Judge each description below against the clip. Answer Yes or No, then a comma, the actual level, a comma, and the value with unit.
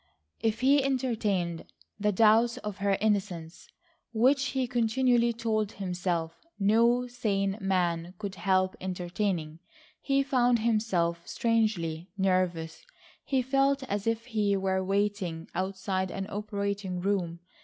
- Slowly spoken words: Yes, slow, 120 wpm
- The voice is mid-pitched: No, high, 200 Hz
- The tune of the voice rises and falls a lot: No, average, 3.8 semitones